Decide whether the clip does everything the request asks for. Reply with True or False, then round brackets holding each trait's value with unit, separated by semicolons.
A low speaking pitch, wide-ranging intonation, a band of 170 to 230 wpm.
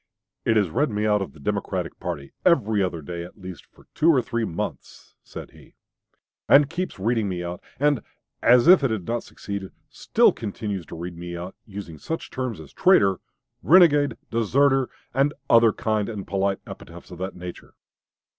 True (105 Hz; 6.0 semitones; 180 wpm)